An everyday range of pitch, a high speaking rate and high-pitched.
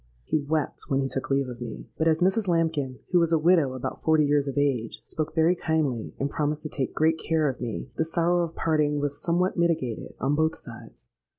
No: average, 3.0 semitones; fast, 220 wpm; medium, 155 Hz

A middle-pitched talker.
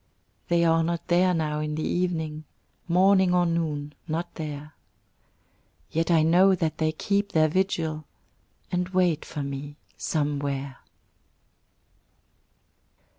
Yes: medium, 160 Hz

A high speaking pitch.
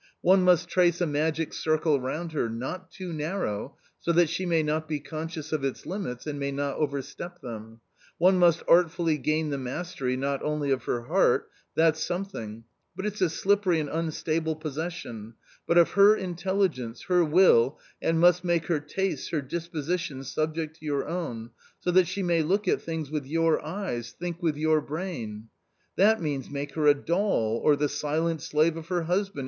No: medium, 160 Hz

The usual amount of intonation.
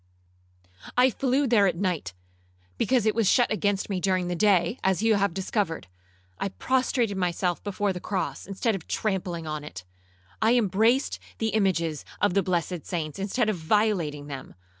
Yes: average, 3.9 semitones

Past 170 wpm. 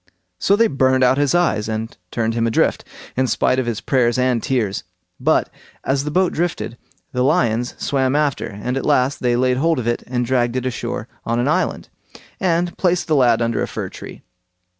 Yes: average, 200 wpm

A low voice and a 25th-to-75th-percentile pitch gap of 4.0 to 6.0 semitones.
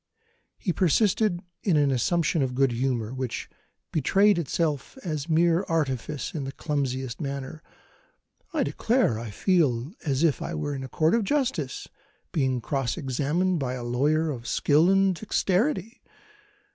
No: medium, 150 Hz; average, 5.0 semitones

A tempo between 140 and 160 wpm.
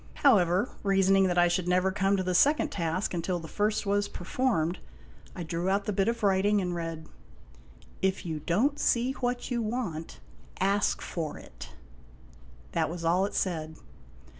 No: average, 170 wpm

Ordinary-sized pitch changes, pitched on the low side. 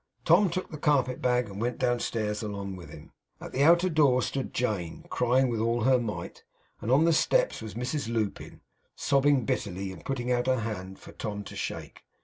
Yes: average, 4.2 semitones; low, 120 Hz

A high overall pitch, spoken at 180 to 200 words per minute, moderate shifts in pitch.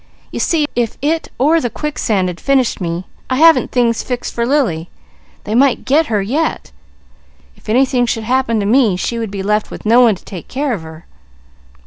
Yes: high, 235 Hz; average, 195 wpm; average, 4.9 semitones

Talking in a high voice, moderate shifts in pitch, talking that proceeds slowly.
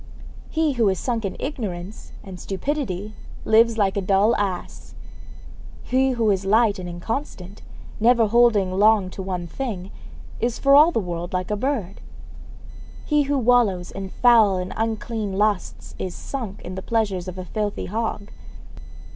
No: high, 210 Hz; average, 3.9 semitones; average, 155 wpm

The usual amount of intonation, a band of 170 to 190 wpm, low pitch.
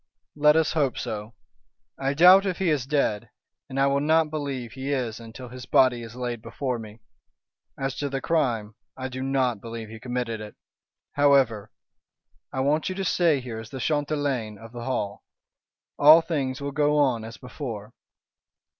Yes: average, 3.9 semitones; average, 175 wpm; low, 130 Hz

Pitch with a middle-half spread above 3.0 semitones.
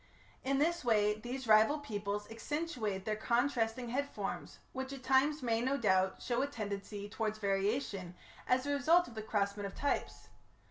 Yes: average, 4.7 semitones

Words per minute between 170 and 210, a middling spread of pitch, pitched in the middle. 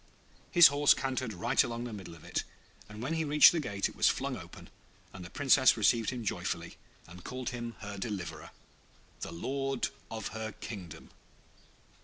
No: average, 180 wpm; average, 4.7 semitones; low, 115 Hz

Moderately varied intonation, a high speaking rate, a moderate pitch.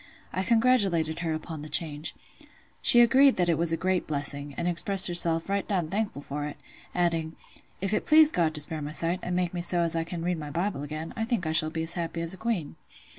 Yes: average, 3.1 semitones; fast, 235 wpm; medium, 170 Hz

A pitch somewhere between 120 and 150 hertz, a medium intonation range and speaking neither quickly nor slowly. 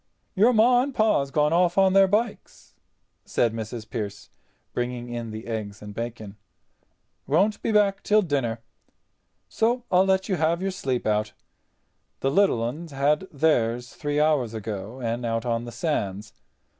No: low, 135 Hz; wide, 8.8 semitones; average, 155 wpm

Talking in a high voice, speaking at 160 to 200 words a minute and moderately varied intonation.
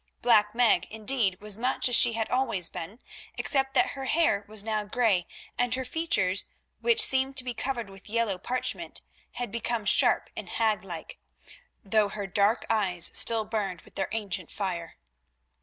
Yes: high, 220 Hz; average, 165 wpm; average, 3.8 semitones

